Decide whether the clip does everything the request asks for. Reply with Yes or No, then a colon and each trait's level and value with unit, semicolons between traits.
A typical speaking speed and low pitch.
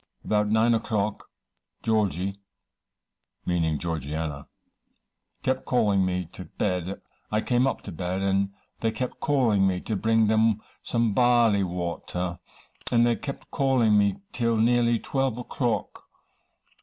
No: slow, 130 wpm; low, 110 Hz